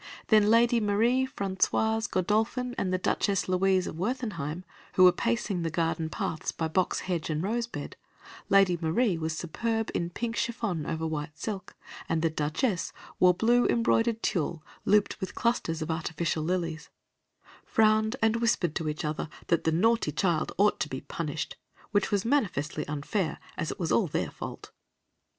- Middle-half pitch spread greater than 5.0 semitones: Yes, wide, 5.6 semitones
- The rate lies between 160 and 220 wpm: Yes, average, 165 wpm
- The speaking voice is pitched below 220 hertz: Yes, medium, 185 Hz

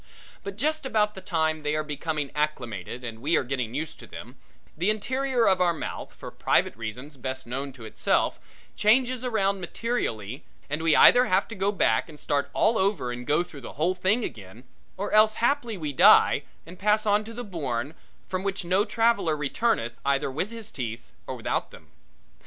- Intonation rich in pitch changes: Yes, wide, 7.7 semitones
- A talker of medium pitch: Yes, medium, 170 Hz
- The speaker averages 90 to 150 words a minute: No, average, 190 wpm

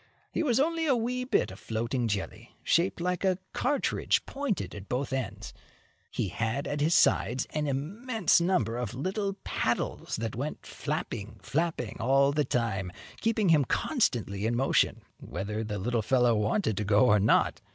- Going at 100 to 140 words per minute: No, average, 165 wpm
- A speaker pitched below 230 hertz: Yes, low, 135 Hz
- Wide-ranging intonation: Yes, wide, 8.7 semitones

